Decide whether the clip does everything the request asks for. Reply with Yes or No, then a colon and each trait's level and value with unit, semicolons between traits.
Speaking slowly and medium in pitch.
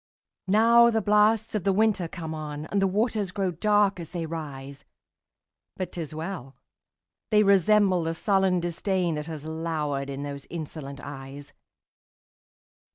Yes: slow, 130 wpm; medium, 175 Hz